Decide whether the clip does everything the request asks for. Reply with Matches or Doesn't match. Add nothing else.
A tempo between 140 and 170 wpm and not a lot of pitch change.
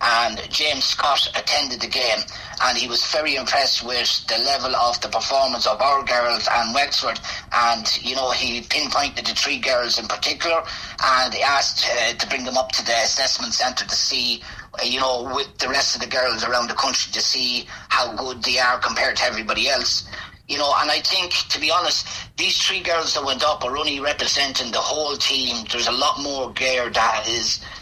Doesn't match